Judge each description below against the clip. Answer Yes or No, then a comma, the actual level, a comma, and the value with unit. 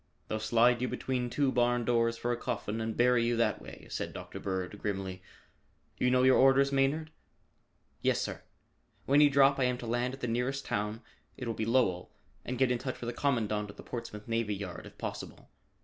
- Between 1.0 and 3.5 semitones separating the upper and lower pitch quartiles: Yes, narrow, 2.6 semitones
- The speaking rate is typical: No, fast, 210 wpm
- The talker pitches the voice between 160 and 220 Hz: No, low, 120 Hz